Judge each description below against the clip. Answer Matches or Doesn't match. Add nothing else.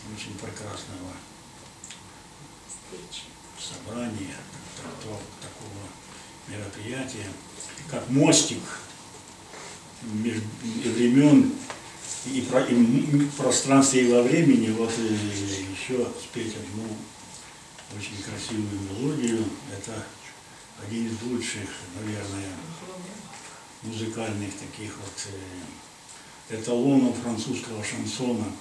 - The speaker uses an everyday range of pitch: Matches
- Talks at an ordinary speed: Doesn't match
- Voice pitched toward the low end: Matches